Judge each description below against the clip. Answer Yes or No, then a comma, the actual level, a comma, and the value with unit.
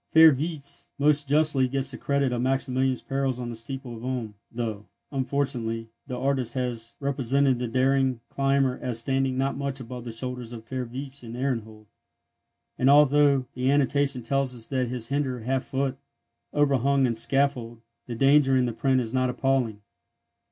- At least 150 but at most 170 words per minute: Yes, average, 165 wpm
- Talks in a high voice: No, low, 130 Hz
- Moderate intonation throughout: No, narrow, 2.2 semitones